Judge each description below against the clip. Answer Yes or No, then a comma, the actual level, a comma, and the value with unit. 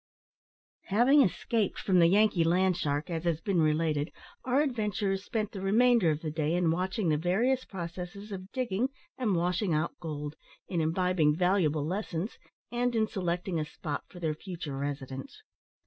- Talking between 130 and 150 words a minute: No, average, 165 wpm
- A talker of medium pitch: Yes, medium, 180 Hz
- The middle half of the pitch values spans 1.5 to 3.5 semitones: No, average, 4.4 semitones